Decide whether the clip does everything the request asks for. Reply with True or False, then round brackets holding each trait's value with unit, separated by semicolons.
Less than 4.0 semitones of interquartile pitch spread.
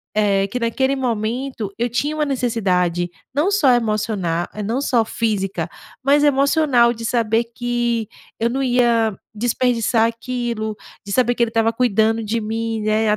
True (2.6 semitones)